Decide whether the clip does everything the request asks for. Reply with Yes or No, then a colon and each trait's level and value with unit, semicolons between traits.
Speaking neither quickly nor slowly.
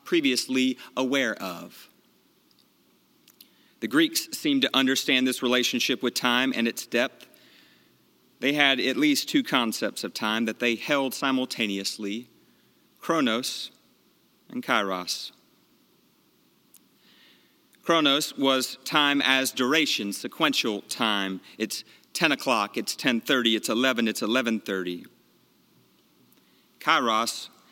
No: slow, 100 wpm